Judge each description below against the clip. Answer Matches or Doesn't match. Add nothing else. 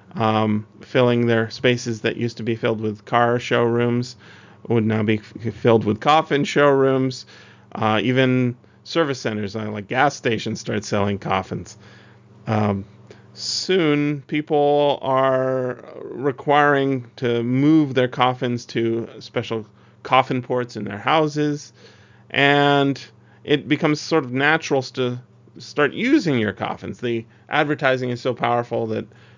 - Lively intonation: Doesn't match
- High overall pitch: Doesn't match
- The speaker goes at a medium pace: Doesn't match